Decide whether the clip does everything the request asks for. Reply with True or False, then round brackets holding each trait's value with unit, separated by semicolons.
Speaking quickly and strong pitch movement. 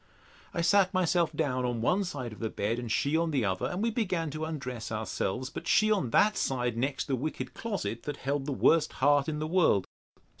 True (220 wpm; 5.8 semitones)